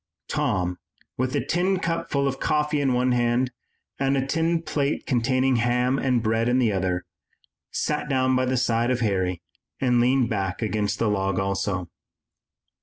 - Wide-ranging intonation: No, average, 4.2 semitones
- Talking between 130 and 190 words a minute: Yes, average, 170 wpm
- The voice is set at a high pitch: No, low, 125 Hz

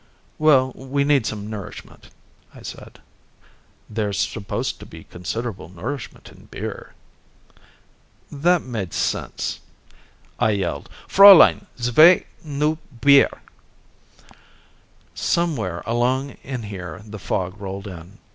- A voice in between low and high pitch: No, low, 115 Hz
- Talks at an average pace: No, slow, 105 wpm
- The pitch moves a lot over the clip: Yes, wide, 6.0 semitones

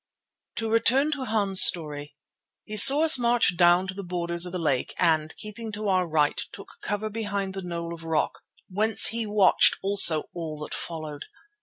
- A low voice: No, high, 190 Hz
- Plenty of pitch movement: No, average, 4.3 semitones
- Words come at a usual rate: Yes, average, 180 wpm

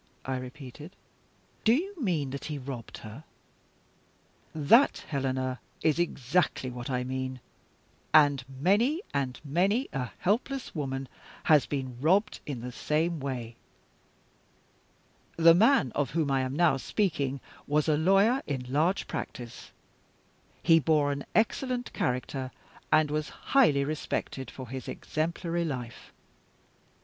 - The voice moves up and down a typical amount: Yes, average, 4.7 semitones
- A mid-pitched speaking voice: Yes, medium, 145 Hz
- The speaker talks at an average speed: No, slow, 125 wpm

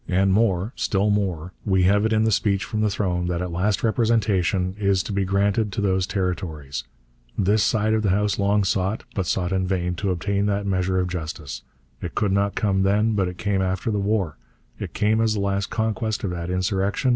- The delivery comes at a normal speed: No, fast, 215 wpm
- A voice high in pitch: No, low, 100 Hz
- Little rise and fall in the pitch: Yes, narrow, 2.2 semitones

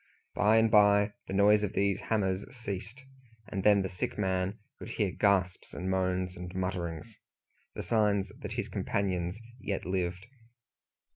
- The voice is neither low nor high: No, very low, 95 Hz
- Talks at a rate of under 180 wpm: Yes, average, 150 wpm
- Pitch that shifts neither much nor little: No, narrow, 2.1 semitones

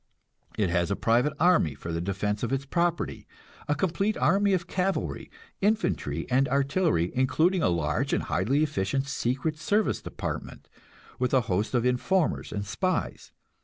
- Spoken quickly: No, average, 155 wpm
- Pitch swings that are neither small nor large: No, wide, 9.0 semitones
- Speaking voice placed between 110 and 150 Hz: Yes, low, 135 Hz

